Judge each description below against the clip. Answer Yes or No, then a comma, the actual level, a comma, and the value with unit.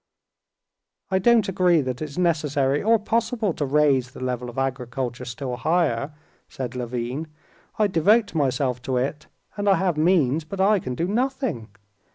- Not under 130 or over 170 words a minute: Yes, average, 160 wpm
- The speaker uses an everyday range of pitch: No, wide, 6.9 semitones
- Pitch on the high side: No, medium, 150 Hz